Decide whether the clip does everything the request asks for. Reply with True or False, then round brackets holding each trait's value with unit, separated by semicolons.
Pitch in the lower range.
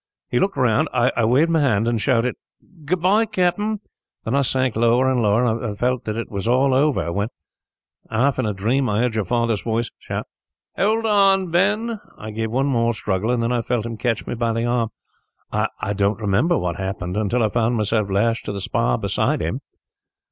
True (120 Hz)